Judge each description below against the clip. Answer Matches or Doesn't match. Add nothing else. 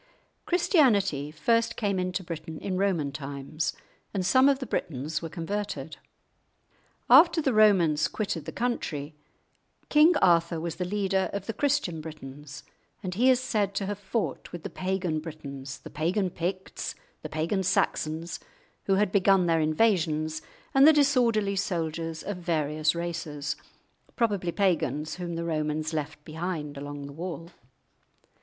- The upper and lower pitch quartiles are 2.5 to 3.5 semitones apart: Doesn't match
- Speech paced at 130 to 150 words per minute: Matches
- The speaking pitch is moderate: Matches